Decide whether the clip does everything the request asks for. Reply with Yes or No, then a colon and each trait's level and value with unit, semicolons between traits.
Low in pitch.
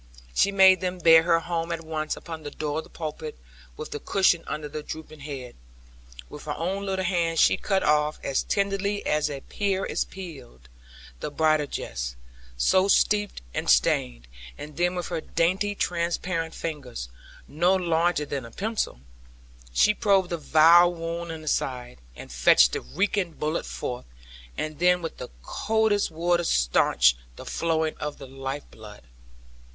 No: medium, 165 Hz